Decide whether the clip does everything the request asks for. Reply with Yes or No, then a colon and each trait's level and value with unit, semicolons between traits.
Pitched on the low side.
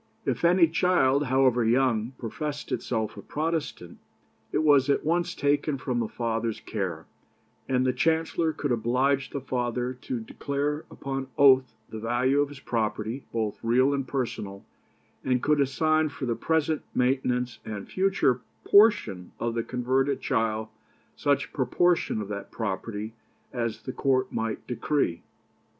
Yes: low, 130 Hz